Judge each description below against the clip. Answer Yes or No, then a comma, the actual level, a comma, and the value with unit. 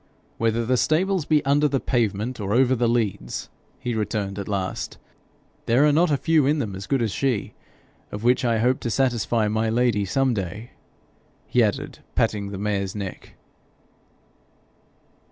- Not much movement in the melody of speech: No, average, 4.4 semitones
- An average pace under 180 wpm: Yes, average, 165 wpm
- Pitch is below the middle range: Yes, low, 115 Hz